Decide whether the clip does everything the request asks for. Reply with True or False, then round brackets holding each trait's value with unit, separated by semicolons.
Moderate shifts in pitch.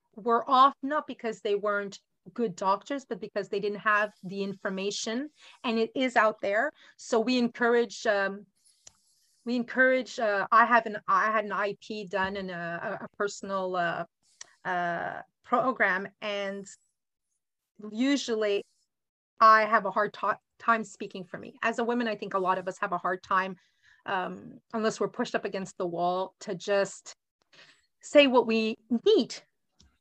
True (3.0 semitones)